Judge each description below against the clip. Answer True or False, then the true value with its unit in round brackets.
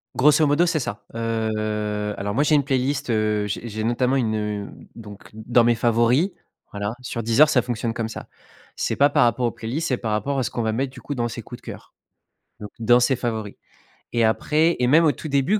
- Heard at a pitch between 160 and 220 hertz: False (120 Hz)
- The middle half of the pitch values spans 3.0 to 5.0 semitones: True (3.8 semitones)